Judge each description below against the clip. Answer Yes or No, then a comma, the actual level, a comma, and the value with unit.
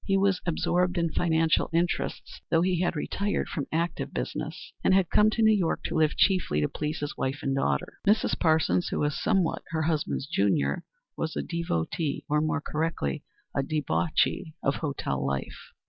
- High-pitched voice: No, medium, 160 Hz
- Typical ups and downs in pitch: Yes, average, 3.8 semitones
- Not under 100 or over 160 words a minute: No, average, 180 wpm